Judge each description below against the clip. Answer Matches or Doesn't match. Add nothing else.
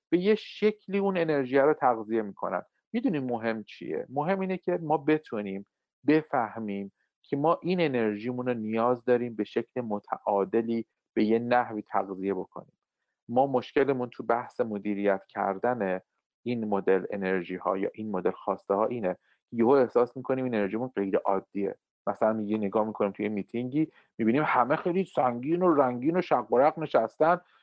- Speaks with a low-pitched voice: Matches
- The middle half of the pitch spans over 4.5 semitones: Matches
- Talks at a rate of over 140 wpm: Matches